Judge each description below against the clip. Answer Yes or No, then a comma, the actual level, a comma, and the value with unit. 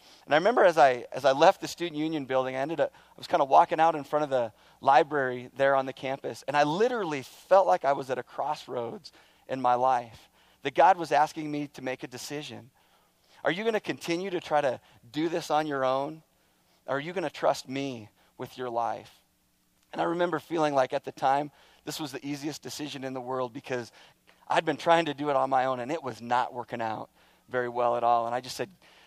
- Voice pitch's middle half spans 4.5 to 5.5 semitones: No, average, 3.4 semitones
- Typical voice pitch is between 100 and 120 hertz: No, low, 135 Hz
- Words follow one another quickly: Yes, fast, 235 wpm